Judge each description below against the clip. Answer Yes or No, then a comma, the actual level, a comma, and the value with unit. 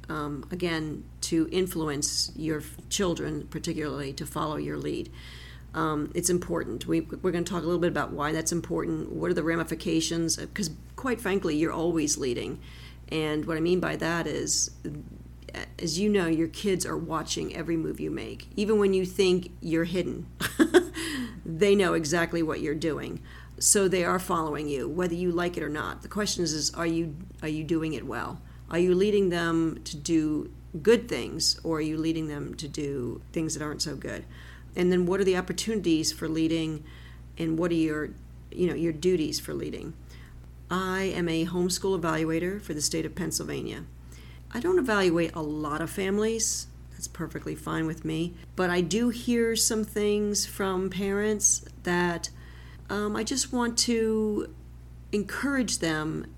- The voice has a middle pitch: Yes, medium, 165 Hz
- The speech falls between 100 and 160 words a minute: No, average, 175 wpm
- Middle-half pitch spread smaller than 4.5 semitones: Yes, average, 3.6 semitones